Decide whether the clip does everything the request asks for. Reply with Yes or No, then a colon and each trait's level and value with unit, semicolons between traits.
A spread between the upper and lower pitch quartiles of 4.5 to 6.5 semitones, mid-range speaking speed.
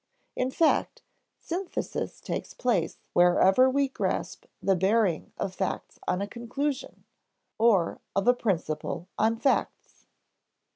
No: wide, 5.5 semitones; slow, 115 wpm